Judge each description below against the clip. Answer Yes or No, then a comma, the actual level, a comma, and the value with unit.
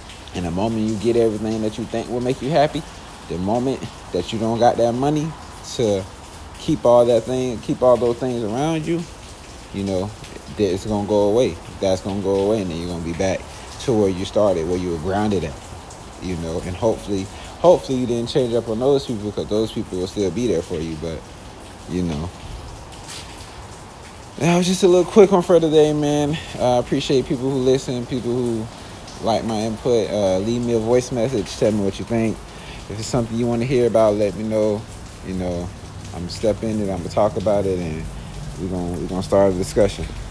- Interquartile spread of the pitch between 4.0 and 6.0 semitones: Yes, average, 4.6 semitones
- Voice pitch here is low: Yes, low, 110 Hz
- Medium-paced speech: No, fast, 215 wpm